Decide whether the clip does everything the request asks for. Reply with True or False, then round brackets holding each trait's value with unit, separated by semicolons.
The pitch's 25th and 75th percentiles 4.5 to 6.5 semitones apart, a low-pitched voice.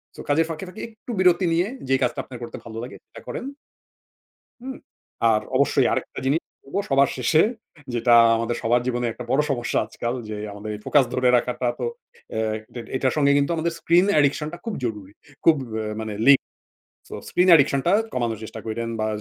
True (5.3 semitones; 130 Hz)